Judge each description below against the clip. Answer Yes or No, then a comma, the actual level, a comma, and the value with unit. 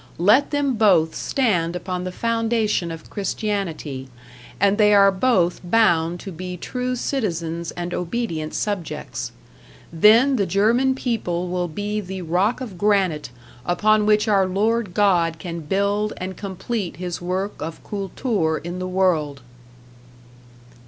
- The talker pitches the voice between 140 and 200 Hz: Yes, high, 190 Hz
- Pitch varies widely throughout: No, average, 3.7 semitones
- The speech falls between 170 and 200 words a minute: No, slow, 135 wpm